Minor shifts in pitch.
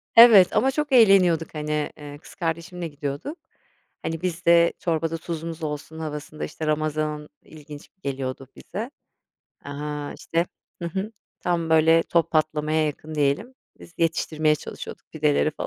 Yes: narrow, 2.2 semitones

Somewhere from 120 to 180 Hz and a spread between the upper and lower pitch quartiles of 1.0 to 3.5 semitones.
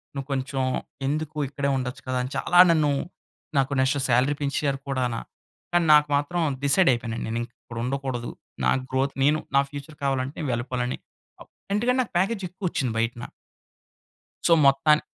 Yes: medium, 140 Hz; average, 2.9 semitones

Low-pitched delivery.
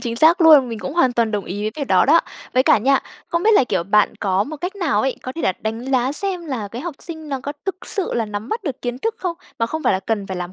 No: very high, 260 Hz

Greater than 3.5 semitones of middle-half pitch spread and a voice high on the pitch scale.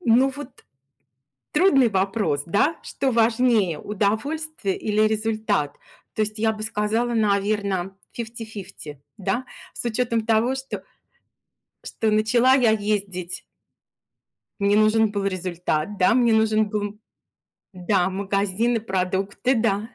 No: average, 2.7 semitones; high, 215 Hz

